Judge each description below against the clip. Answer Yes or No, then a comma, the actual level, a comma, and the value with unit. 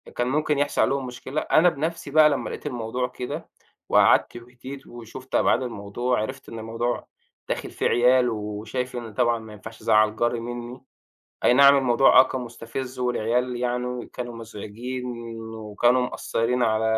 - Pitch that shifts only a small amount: Yes, narrow, 2.0 semitones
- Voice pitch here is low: Yes, low, 125 Hz